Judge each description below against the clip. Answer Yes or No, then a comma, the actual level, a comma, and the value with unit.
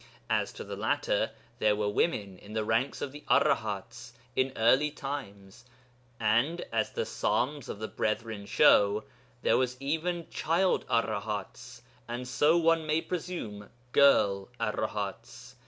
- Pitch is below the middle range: Yes, low, 120 Hz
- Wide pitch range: Yes, wide, 6.1 semitones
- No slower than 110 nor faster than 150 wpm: Yes, average, 140 wpm